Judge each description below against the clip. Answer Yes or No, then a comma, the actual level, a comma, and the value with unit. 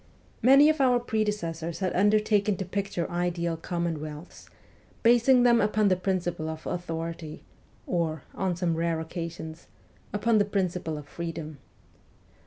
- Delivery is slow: Yes, slow, 130 wpm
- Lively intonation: No, average, 4.0 semitones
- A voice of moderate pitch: Yes, medium, 175 Hz